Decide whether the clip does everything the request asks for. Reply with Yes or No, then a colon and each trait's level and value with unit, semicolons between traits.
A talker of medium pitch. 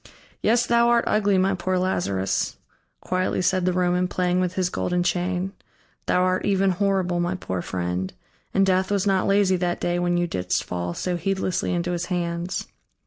Yes: medium, 180 Hz